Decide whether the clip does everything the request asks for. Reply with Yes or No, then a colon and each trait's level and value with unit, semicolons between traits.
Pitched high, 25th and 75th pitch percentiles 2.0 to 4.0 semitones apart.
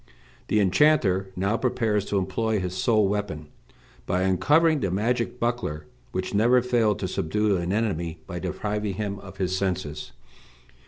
No: low, 100 Hz; average, 3.4 semitones